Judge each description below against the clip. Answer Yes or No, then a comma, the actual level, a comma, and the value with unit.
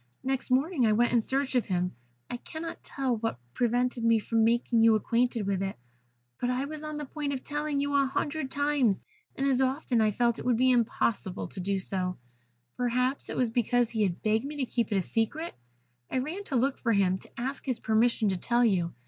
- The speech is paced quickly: Yes, fast, 220 wpm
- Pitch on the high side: Yes, high, 245 Hz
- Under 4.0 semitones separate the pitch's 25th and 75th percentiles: Yes, average, 3.6 semitones